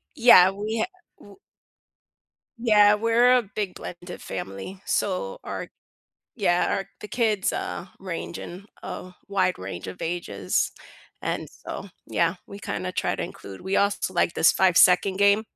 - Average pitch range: Yes, average, 3.1 semitones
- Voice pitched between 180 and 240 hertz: Yes, high, 190 Hz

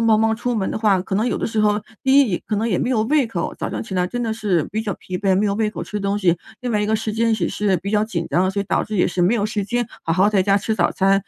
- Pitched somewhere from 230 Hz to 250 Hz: No, high, 210 Hz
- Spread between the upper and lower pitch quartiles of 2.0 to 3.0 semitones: Yes, narrow, 2.5 semitones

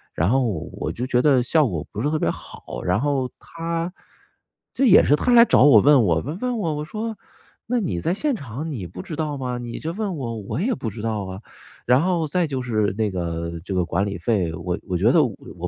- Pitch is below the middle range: Yes, low, 125 Hz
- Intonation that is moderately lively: No, wide, 8.9 semitones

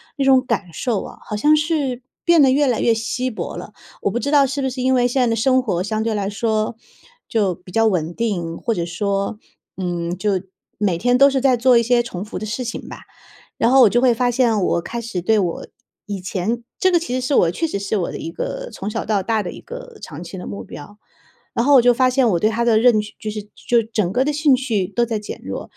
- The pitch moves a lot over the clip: No, average, 4.3 semitones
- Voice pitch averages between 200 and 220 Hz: No, high, 230 Hz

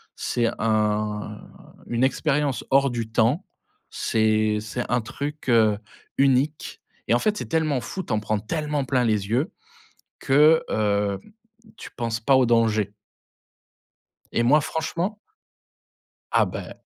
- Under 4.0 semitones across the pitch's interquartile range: No, average, 5.0 semitones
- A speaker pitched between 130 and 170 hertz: No, low, 120 Hz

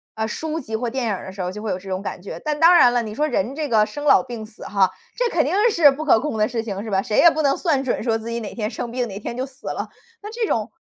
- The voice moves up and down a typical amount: No, wide, 5.7 semitones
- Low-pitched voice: No, high, 235 Hz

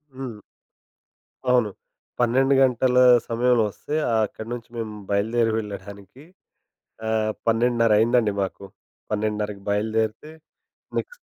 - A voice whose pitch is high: No, low, 115 Hz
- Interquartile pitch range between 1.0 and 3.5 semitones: Yes, average, 2.8 semitones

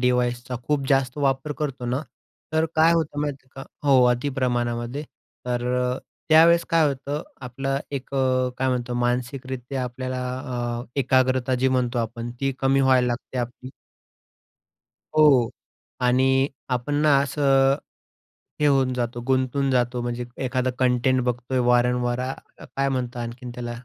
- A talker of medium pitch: No, low, 130 Hz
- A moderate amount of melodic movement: No, narrow, 1.8 semitones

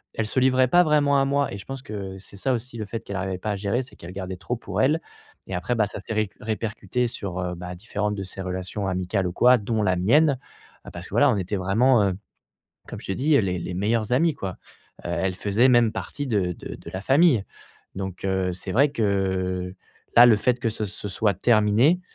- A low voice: Yes, low, 105 Hz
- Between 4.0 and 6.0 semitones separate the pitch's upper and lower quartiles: Yes, average, 4.6 semitones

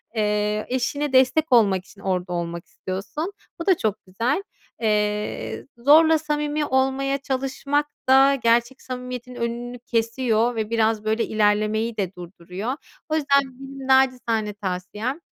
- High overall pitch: Yes, high, 235 Hz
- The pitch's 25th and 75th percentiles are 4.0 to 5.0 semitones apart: Yes, average, 4.3 semitones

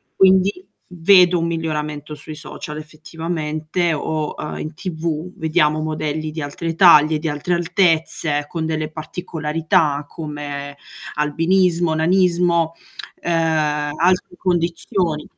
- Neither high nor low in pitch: Yes, medium, 160 Hz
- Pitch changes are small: Yes, narrow, 2.2 semitones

